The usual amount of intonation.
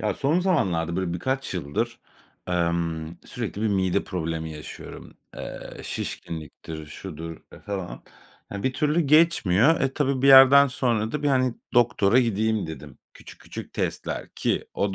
No: wide, 7.9 semitones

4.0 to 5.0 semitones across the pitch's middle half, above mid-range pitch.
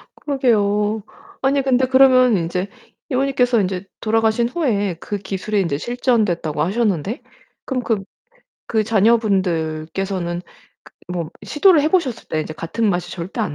No: wide, 5.5 semitones; high, 215 Hz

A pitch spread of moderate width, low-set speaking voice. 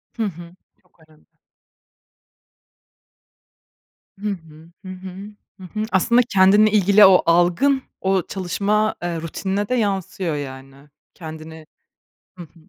No: average, 3.9 semitones; medium, 185 Hz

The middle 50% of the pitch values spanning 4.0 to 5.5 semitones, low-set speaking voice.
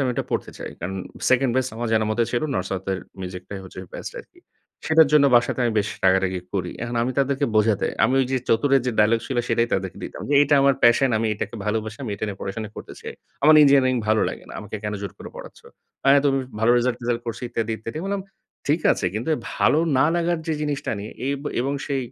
Yes: average, 4.5 semitones; low, 120 Hz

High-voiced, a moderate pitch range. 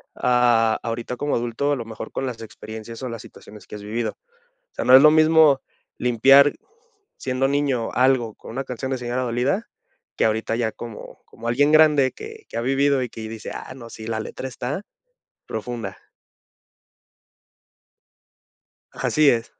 No: low, 125 Hz; average, 3.2 semitones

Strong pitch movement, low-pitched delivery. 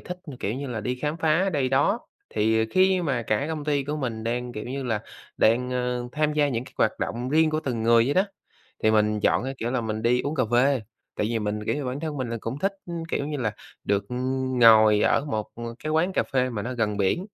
No: average, 4.7 semitones; low, 125 Hz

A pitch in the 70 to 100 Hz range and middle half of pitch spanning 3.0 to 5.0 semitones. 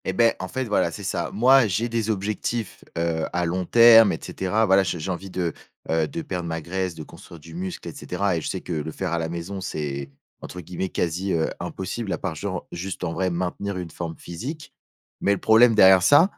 Yes: very low, 95 Hz; average, 3.9 semitones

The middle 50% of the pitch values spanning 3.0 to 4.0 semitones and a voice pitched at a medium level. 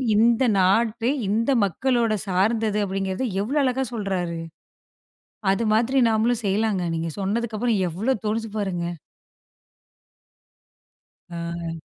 No: average, 3.6 semitones; high, 215 Hz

